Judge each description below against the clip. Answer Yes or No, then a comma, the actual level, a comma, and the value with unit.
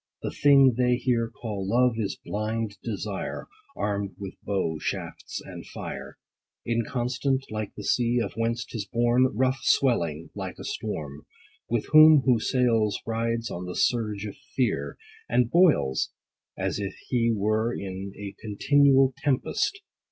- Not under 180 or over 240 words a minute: No, average, 145 wpm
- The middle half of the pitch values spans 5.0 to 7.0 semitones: No, average, 3.6 semitones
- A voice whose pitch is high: No, low, 115 Hz